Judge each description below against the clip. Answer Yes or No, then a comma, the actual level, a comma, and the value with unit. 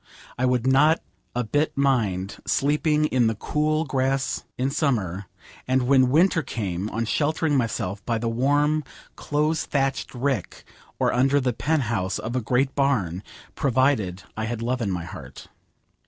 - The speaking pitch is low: Yes, low, 130 Hz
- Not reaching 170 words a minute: Yes, average, 155 wpm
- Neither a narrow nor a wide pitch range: Yes, average, 4.2 semitones